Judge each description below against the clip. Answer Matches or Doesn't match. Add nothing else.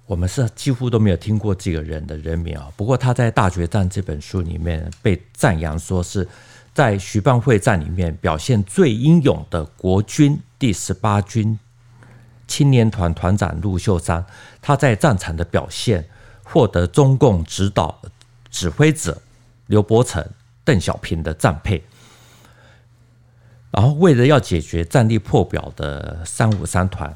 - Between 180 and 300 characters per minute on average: Matches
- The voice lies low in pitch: Matches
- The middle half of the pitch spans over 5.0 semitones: Matches